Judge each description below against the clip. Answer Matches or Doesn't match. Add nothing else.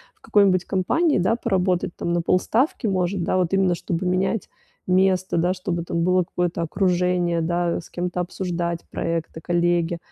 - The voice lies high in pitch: Doesn't match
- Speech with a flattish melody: Matches